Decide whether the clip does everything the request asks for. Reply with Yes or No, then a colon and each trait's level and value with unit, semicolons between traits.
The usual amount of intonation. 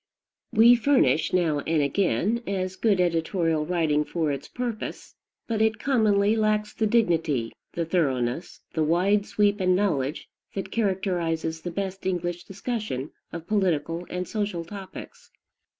Yes: average, 4.3 semitones